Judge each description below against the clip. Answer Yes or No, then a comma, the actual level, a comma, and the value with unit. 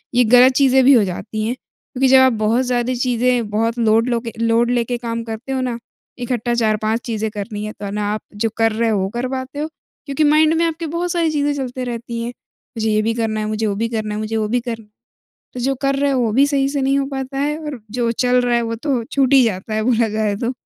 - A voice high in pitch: Yes, high, 240 Hz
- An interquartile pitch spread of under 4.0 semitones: Yes, average, 3.2 semitones